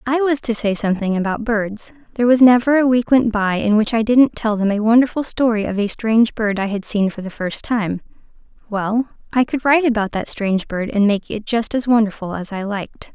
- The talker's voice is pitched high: Yes, high, 225 Hz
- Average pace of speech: No, fast, 235 wpm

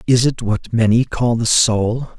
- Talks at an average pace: Yes, average, 190 wpm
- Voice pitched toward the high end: No, low, 115 Hz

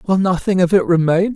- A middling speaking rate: No, fast, 220 wpm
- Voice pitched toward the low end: No, medium, 180 Hz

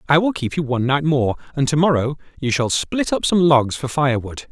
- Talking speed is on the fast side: Yes, fast, 240 wpm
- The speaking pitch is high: No, medium, 140 Hz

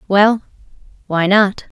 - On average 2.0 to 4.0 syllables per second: Yes, 3.4 syllables/s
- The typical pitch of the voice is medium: No, high, 200 Hz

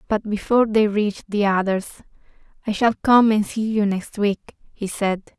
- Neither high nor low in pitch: No, high, 210 Hz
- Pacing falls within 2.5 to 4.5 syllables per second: No, 5.1 syllables/s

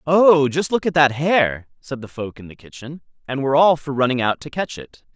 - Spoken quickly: Yes, fast, 245 wpm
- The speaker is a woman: No, male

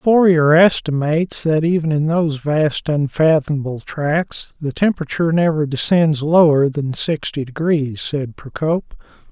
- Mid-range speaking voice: Yes, medium, 155 Hz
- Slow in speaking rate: Yes, slow, 120 wpm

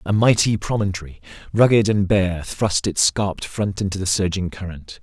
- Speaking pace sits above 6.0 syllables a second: No, 5.0 syllables/s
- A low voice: Yes, very low, 95 Hz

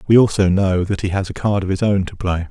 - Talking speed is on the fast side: Yes, fast, 310 wpm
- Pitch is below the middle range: Yes, very low, 95 Hz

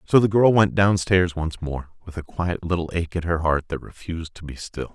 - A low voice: Yes, very low, 85 Hz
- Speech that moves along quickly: Yes, fast, 245 wpm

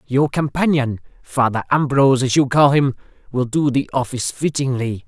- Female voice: No, male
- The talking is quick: No, average, 155 wpm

